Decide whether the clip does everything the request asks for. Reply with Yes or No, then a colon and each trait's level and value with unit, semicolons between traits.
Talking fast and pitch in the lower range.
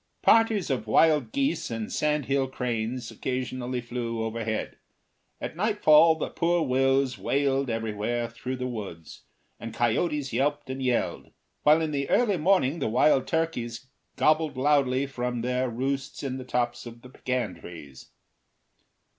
No: average, 140 wpm; low, 130 Hz